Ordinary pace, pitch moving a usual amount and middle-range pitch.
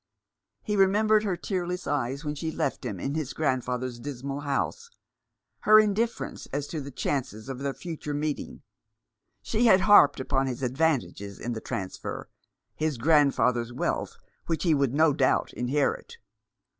Yes: average, 150 wpm; average, 5.0 semitones; medium, 145 Hz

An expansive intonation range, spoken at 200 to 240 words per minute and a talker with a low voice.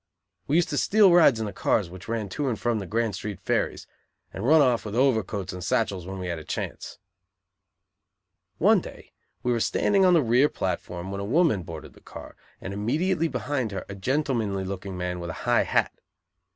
Yes: wide, 6.3 semitones; fast, 205 wpm; low, 110 Hz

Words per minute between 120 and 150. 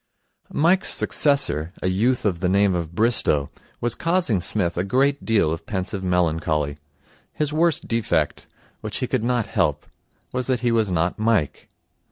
No: average, 160 wpm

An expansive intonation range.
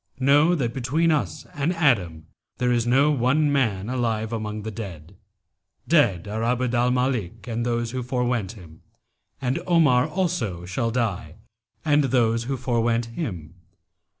No: average, 3.9 semitones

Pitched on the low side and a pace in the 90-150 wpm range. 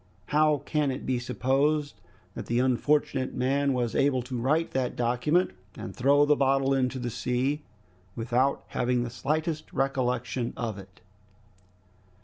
Yes: low, 130 Hz; average, 140 wpm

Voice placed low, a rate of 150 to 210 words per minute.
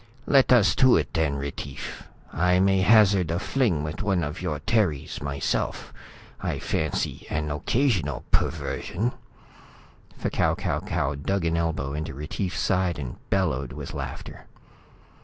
No: very low, 85 Hz; average, 140 wpm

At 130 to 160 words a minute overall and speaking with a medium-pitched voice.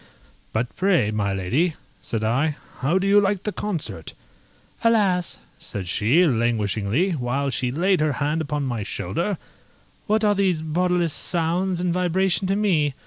Yes: average, 150 wpm; medium, 160 Hz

